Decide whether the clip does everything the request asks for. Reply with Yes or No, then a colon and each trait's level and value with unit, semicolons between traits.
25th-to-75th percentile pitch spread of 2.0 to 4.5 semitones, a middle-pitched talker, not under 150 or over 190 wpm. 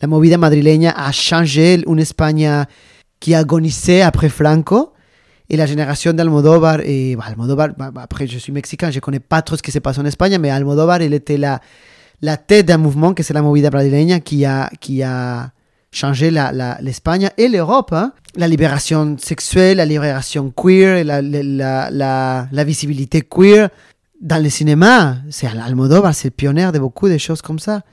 Yes: average, 3.1 semitones; medium, 150 Hz; average, 175 wpm